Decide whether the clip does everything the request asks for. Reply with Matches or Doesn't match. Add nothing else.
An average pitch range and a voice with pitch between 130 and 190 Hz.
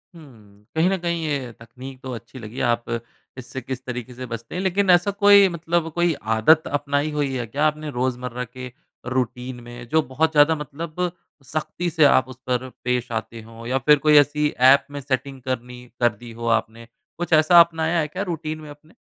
Matches